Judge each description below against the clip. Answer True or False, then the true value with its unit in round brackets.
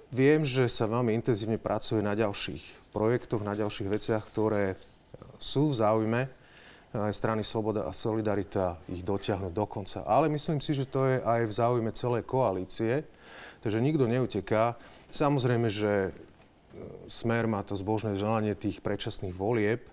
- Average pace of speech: True (145 wpm)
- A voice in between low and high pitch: False (110 Hz)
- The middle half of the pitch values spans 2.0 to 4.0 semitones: True (2.6 semitones)